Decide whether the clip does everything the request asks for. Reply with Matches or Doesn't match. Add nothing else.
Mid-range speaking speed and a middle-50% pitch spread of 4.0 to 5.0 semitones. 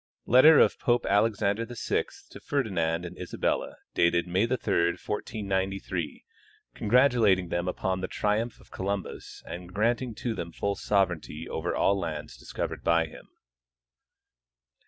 Doesn't match